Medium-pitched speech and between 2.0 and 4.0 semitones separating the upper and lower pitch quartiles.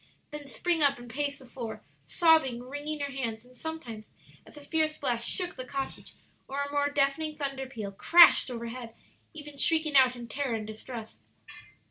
No: very high, 275 Hz; average, 3.6 semitones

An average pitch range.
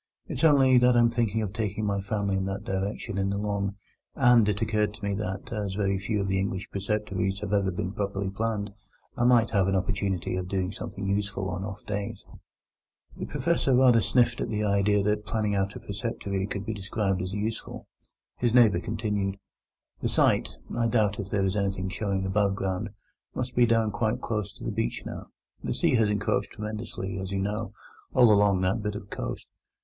No: narrow, 1.9 semitones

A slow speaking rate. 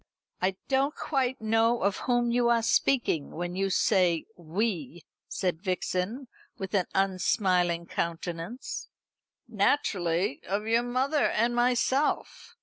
Yes: slow, 120 wpm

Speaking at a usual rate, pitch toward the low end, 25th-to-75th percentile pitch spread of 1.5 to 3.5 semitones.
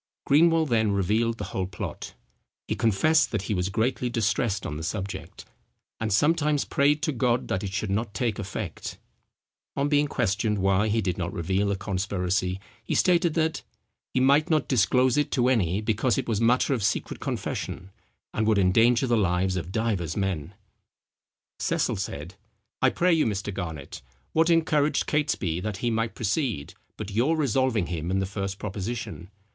No: average, 170 wpm; low, 110 Hz; wide, 5.4 semitones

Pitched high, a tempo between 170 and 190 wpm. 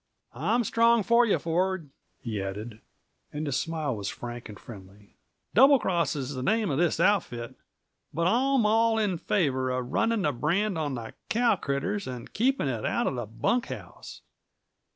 No: medium, 165 Hz; average, 175 wpm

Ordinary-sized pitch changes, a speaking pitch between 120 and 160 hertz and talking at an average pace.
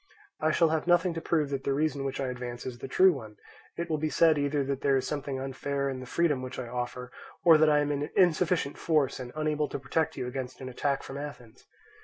No: average, 3.2 semitones; medium, 140 Hz; fast, 245 wpm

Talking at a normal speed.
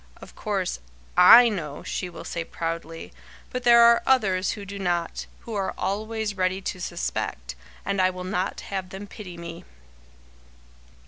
Yes: average, 155 wpm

